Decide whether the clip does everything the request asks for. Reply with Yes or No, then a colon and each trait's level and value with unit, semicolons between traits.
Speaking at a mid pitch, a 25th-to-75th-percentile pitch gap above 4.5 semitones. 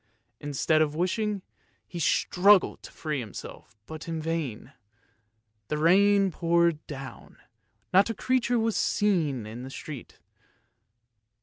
Yes: medium, 165 Hz; average, 5.1 semitones